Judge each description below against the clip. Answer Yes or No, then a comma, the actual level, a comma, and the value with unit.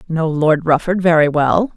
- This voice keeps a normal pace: Yes, average, 170 wpm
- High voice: No, medium, 165 Hz